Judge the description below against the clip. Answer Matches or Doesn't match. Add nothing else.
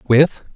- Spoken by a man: Matches